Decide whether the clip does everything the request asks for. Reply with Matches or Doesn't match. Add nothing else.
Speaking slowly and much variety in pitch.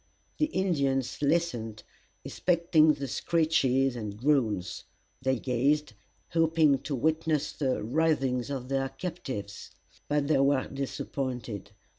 Doesn't match